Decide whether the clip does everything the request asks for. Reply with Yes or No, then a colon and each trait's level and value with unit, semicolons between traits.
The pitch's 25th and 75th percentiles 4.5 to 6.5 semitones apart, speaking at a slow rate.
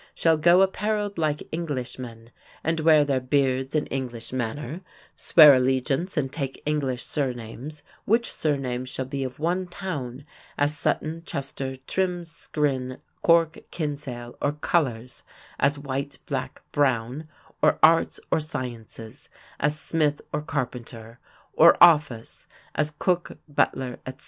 No: average, 3.8 semitones; slow, 130 wpm